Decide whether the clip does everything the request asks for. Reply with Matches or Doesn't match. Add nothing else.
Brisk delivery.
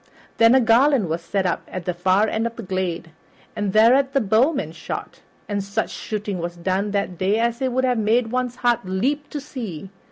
Matches